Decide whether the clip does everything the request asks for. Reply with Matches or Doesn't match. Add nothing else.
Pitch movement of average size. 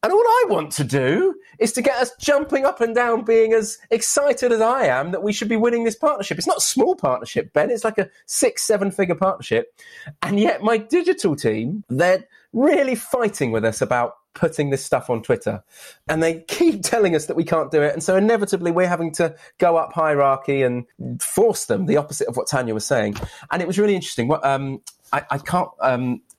Doesn't match